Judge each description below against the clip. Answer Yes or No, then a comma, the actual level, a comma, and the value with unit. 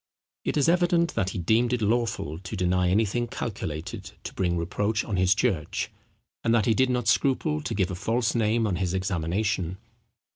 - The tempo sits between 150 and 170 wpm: No, average, 185 wpm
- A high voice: No, low, 105 Hz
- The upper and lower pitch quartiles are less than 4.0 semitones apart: No, average, 4.5 semitones